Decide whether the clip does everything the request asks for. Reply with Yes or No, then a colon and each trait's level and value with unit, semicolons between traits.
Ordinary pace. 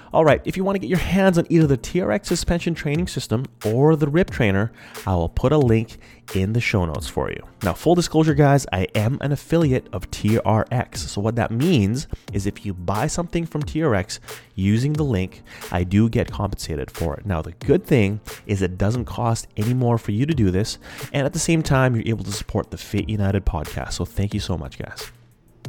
No: fast, 220 wpm